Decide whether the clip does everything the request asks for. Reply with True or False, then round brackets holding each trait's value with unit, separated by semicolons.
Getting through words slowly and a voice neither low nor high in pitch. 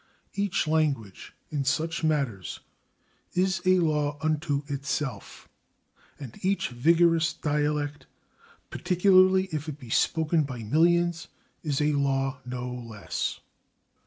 True (120 wpm; 150 Hz)